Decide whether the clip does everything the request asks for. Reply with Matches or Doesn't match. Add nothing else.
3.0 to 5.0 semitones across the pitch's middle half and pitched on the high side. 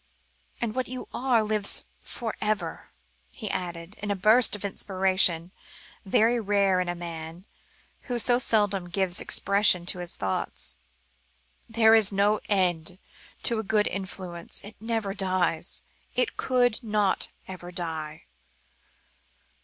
Matches